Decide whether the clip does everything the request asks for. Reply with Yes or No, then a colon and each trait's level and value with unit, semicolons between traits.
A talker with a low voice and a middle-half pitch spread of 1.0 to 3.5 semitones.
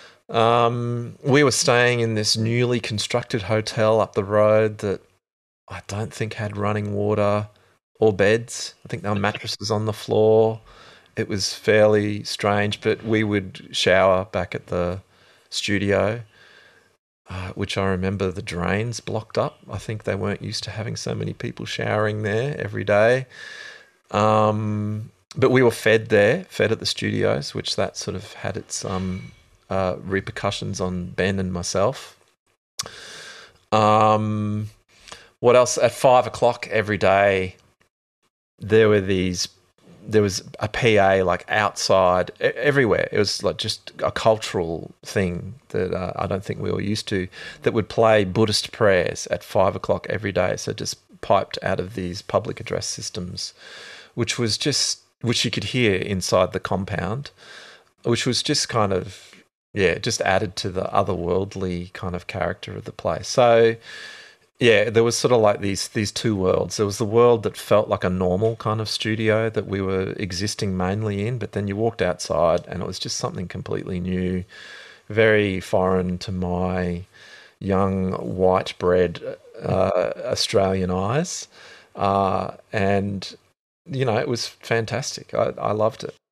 Yes: low, 105 Hz; average, 3.0 semitones